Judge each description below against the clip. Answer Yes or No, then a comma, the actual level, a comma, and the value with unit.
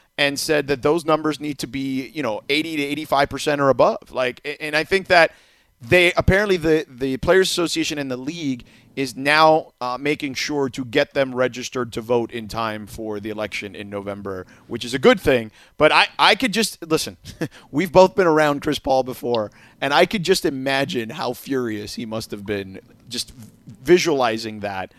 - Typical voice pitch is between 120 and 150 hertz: Yes, low, 135 Hz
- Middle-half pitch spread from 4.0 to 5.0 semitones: Yes, average, 4.6 semitones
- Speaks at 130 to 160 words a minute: No, average, 190 wpm